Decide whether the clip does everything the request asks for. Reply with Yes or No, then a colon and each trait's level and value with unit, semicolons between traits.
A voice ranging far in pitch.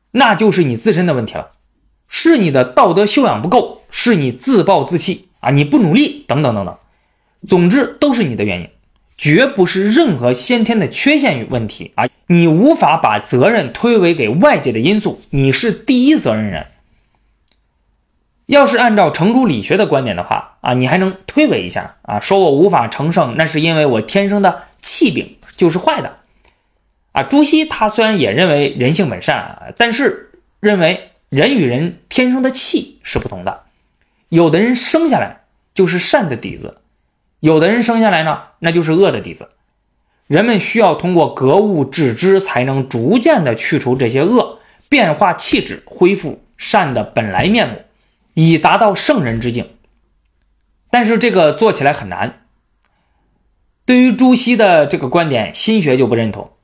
Yes: wide, 9.0 semitones